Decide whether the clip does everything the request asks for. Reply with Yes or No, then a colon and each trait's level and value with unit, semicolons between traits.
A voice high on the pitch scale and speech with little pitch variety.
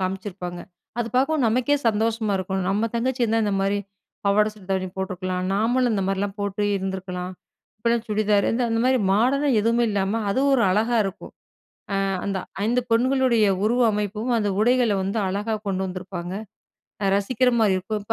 No: high, 210 Hz; average, 3.4 semitones